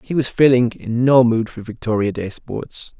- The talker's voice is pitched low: Yes, low, 120 Hz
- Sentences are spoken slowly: No, average, 200 wpm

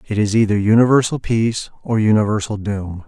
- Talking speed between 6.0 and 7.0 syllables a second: No, 5.7 syllables/s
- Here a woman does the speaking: No, male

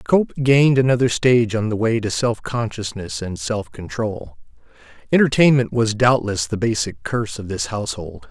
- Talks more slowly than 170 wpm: Yes, average, 160 wpm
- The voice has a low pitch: Yes, low, 110 Hz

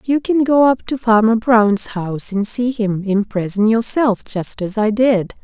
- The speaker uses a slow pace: No, average, 200 wpm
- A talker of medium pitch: No, high, 220 Hz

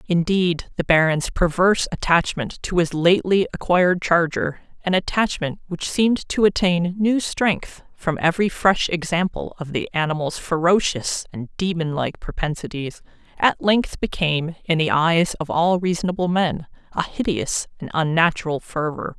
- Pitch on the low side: No, medium, 170 Hz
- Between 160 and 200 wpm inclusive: No, slow, 135 wpm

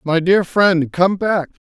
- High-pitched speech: No, medium, 175 Hz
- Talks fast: No, average, 180 wpm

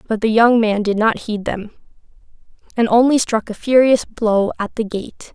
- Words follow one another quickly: No, average, 190 wpm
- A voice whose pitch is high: Yes, high, 220 Hz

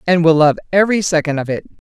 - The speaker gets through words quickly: Yes, fast, 220 wpm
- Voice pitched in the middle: Yes, medium, 165 Hz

